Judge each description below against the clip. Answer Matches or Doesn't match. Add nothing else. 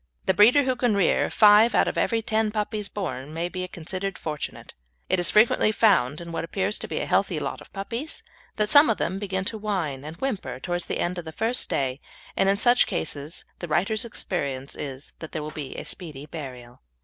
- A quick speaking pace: Matches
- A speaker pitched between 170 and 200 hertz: Matches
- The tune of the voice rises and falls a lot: Matches